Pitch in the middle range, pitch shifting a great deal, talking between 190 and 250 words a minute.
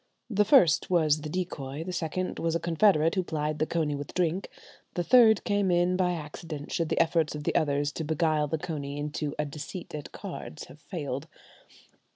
No: medium, 160 Hz; average, 3.1 semitones; average, 195 wpm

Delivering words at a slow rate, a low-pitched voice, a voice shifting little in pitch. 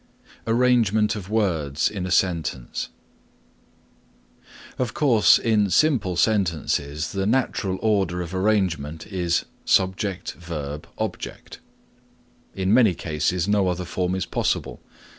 No: slow, 110 wpm; very low, 95 Hz; average, 3.8 semitones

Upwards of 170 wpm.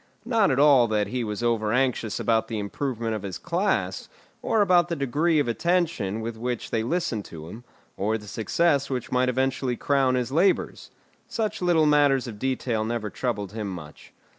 Yes: average, 185 wpm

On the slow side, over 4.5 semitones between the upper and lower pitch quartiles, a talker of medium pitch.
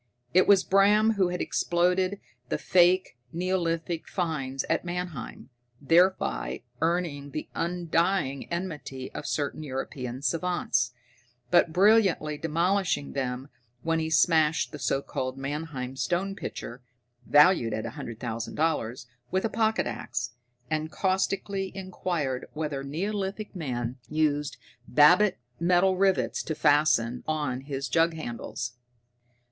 Yes: slow, 120 wpm; average, 5.1 semitones; medium, 160 Hz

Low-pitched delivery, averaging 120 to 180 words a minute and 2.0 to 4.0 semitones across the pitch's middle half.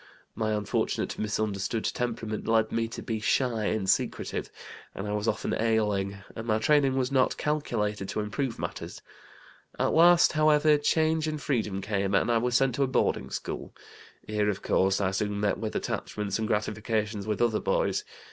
Yes: low, 110 Hz; average, 175 wpm; average, 3.5 semitones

